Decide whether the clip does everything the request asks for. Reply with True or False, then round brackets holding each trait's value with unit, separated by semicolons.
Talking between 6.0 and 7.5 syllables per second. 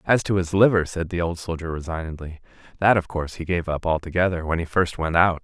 True (6.1 syllables/s)